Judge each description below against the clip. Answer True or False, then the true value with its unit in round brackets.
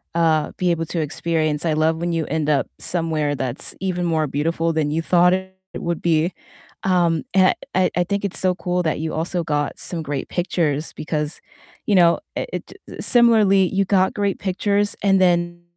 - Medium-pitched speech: True (170 Hz)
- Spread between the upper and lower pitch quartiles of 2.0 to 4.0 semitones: True (2.9 semitones)